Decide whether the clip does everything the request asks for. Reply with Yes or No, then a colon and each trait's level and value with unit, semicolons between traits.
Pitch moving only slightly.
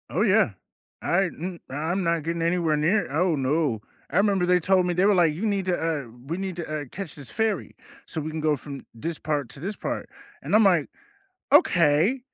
No: average, 3.6 semitones